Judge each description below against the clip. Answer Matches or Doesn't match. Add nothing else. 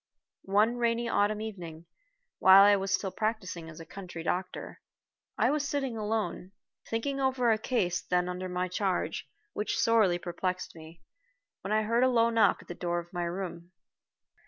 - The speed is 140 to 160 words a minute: Doesn't match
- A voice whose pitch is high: Matches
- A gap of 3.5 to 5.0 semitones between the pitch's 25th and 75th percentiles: Matches